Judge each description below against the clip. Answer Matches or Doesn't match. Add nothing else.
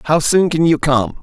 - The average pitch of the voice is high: Doesn't match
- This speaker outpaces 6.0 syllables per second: Doesn't match